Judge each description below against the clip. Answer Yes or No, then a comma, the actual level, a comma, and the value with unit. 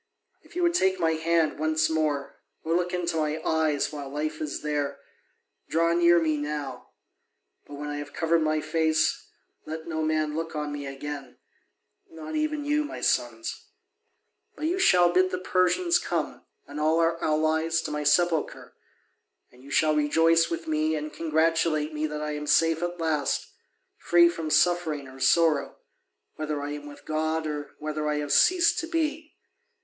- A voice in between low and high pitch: Yes, medium, 155 Hz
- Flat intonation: Yes, narrow, 2.1 semitones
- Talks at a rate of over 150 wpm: Yes, average, 175 wpm